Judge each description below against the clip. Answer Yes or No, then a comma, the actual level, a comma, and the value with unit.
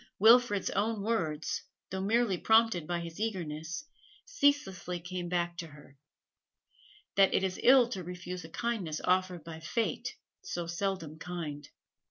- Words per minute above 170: No, average, 140 wpm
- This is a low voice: No, medium, 180 Hz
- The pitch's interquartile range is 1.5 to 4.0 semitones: No, average, 4.5 semitones